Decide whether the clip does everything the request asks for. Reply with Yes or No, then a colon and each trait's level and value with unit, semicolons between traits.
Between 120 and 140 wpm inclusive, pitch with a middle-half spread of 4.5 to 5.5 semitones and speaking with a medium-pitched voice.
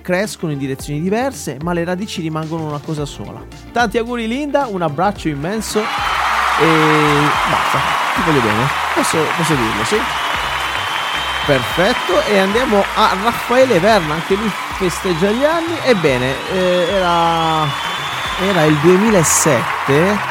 Yes: average, 125 wpm; average, 5.2 semitones; medium, 180 Hz